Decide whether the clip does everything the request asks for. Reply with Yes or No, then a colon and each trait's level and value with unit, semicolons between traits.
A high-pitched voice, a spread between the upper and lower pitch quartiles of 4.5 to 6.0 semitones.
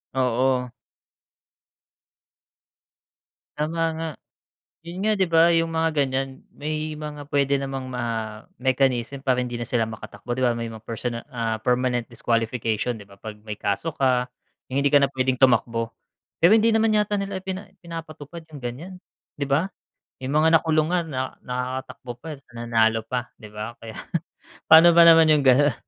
No: low, 130 Hz; average, 5.1 semitones